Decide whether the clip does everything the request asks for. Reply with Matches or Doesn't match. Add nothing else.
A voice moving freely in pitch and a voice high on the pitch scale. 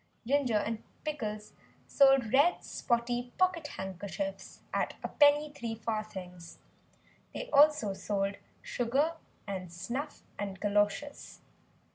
Matches